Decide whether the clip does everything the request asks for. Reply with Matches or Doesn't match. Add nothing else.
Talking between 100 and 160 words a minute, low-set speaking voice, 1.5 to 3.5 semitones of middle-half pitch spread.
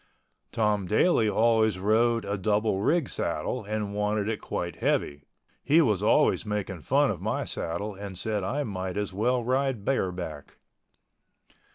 Matches